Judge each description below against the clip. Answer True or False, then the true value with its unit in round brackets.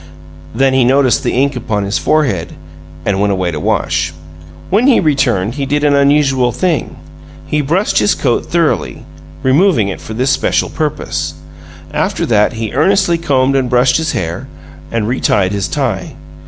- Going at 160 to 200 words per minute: True (165 wpm)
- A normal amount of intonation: False (6.3 semitones)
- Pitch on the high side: False (130 Hz)